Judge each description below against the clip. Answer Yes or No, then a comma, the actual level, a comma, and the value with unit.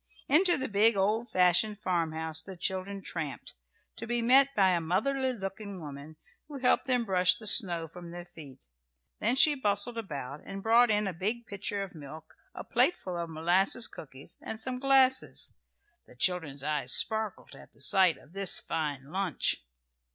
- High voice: Yes, high, 195 Hz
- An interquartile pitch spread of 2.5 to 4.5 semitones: No, wide, 5.6 semitones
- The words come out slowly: No, average, 170 wpm